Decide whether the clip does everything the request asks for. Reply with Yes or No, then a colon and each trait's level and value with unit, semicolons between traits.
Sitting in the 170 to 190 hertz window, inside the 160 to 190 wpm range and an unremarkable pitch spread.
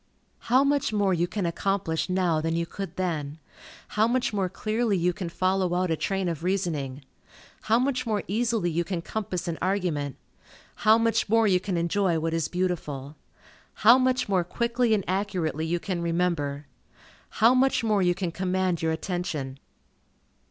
Yes: medium, 185 Hz; average, 170 wpm; average, 4.0 semitones